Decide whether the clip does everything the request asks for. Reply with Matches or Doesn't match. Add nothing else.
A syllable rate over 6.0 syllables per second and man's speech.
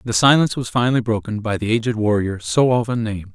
Matches